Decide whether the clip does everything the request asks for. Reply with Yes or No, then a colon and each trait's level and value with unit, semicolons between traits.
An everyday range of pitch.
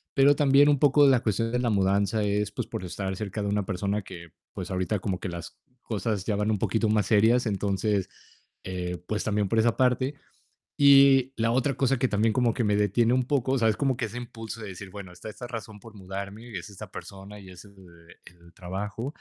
Yes: average, 3.7 semitones